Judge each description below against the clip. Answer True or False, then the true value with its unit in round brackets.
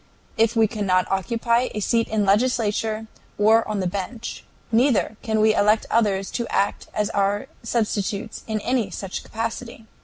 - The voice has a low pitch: False (220 Hz)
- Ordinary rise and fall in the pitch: False (2.1 semitones)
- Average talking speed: True (160 wpm)